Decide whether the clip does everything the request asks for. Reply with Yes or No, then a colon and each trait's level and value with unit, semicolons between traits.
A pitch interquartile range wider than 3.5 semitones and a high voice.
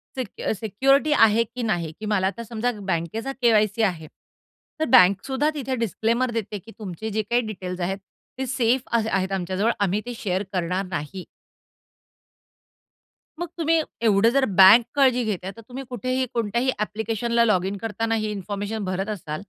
Yes: average, 3.9 semitones; high, 215 Hz